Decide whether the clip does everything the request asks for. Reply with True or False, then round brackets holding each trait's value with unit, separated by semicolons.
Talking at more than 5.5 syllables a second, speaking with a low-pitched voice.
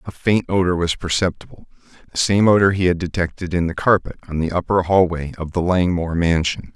True (5.8 syllables/s; 90 Hz)